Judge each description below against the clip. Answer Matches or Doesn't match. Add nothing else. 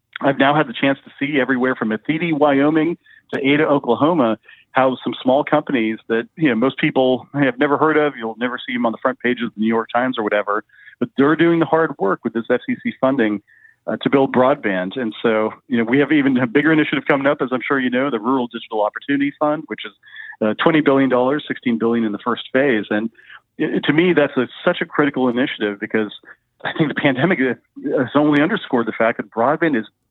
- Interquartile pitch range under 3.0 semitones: Doesn't match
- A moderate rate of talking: Doesn't match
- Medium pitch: Doesn't match